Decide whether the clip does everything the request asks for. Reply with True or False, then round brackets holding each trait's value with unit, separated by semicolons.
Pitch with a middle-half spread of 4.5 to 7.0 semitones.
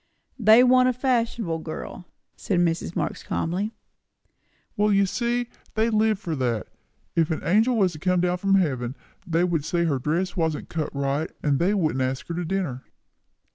True (5.1 semitones)